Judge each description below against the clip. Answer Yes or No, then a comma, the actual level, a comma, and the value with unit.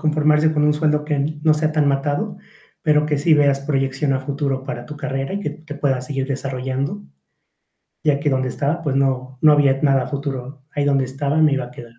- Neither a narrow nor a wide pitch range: No, narrow, 2.0 semitones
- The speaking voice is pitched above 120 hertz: Yes, medium, 140 Hz